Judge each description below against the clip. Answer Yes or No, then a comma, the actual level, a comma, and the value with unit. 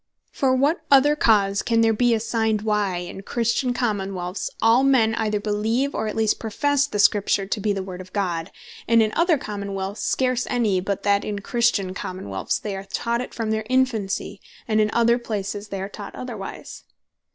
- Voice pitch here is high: Yes, high, 215 Hz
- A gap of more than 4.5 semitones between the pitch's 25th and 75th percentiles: No, average, 3.1 semitones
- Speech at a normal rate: Yes, average, 195 wpm